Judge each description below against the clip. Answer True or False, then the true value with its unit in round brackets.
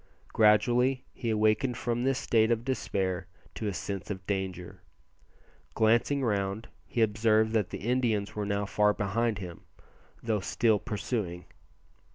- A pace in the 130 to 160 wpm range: True (140 wpm)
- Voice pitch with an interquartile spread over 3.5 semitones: False (2.8 semitones)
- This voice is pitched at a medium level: False (110 Hz)